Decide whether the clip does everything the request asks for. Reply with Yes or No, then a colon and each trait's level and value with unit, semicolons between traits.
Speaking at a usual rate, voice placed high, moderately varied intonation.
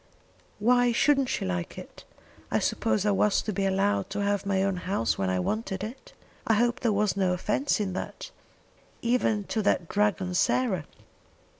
Yes: average, 175 wpm; high, 205 Hz; average, 3.1 semitones